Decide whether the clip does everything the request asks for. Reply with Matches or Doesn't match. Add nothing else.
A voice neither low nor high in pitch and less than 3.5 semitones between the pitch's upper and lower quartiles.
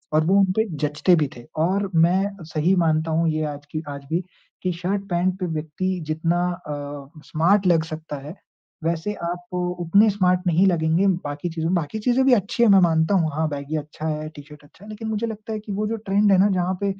Doesn't match